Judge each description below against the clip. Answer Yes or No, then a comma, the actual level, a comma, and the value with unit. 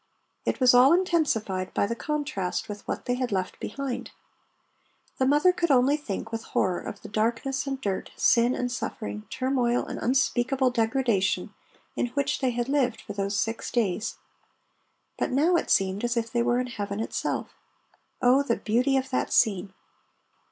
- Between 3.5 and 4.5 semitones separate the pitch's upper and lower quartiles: Yes, average, 3.9 semitones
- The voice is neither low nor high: No, high, 245 Hz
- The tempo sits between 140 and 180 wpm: Yes, average, 170 wpm